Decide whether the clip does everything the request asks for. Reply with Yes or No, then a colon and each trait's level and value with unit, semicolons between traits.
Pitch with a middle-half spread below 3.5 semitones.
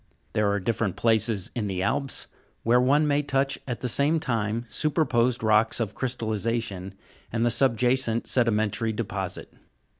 Yes: average, 3.1 semitones